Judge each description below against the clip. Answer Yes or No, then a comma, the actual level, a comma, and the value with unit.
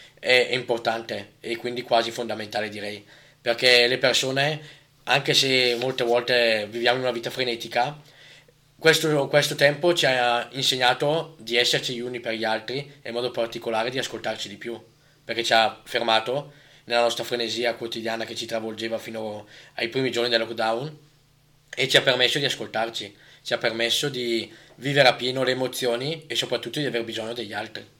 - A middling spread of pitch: Yes, average, 3.5 semitones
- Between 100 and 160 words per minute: No, fast, 170 wpm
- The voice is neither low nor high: No, low, 120 Hz